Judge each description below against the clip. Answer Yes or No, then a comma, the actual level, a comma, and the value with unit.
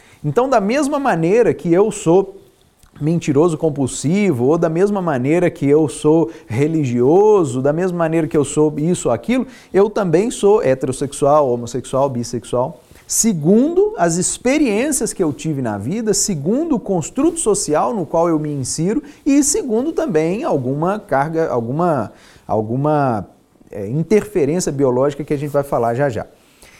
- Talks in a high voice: No, medium, 165 Hz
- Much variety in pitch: Yes, wide, 6.5 semitones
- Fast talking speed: No, average, 145 wpm